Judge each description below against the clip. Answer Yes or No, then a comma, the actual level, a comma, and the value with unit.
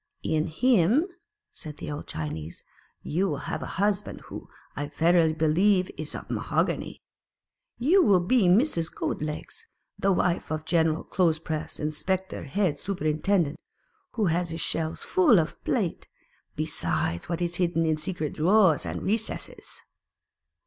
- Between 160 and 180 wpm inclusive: No, average, 145 wpm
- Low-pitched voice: No, medium, 170 Hz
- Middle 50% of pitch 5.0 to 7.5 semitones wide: No, average, 3.8 semitones